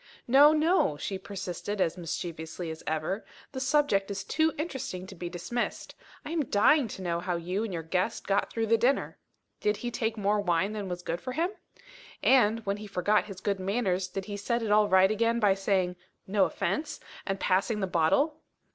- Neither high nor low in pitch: No, high, 200 Hz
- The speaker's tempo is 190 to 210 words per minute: Yes, average, 200 wpm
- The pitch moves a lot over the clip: No, average, 4.1 semitones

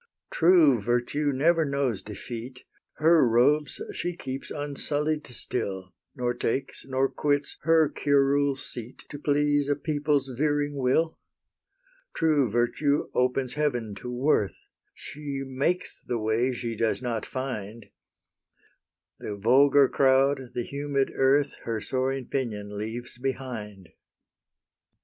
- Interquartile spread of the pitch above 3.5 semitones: No, average, 3.2 semitones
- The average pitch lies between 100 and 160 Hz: Yes, low, 135 Hz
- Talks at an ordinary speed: No, slow, 115 wpm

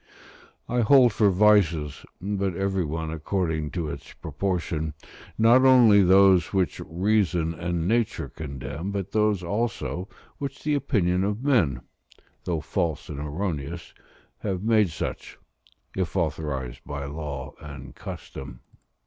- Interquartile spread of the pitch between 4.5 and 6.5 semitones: Yes, average, 5.1 semitones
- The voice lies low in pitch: Yes, very low, 90 Hz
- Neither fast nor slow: No, slow, 125 wpm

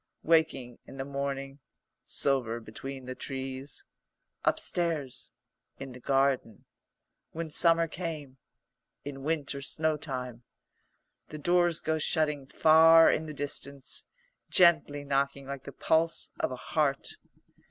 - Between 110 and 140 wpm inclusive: Yes, slow, 135 wpm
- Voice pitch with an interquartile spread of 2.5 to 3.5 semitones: Yes, average, 3.0 semitones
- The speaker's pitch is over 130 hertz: Yes, medium, 140 Hz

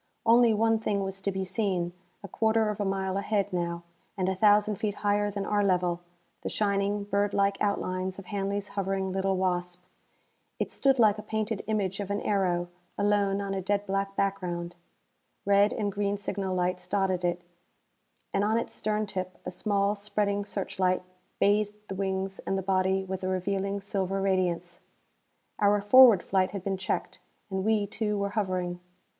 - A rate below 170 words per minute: No, average, 175 wpm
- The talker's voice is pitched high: Yes, high, 195 Hz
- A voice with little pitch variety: Yes, narrow, 1.5 semitones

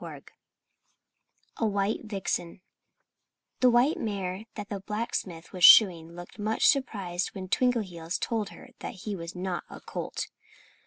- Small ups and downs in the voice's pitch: No, average, 3.6 semitones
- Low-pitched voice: No, high, 195 Hz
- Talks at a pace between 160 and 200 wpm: No, slow, 135 wpm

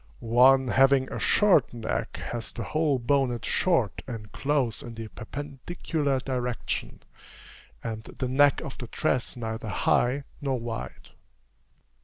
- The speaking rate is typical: No, slow, 130 wpm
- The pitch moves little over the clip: No, average, 3.3 semitones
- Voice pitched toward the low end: Yes, low, 125 Hz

